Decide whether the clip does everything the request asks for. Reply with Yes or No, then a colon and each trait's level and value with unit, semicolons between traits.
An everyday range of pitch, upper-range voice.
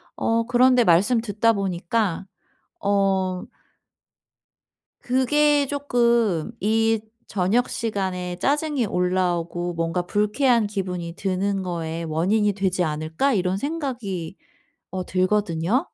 Yes: average, 4.7 semitones; high, 195 Hz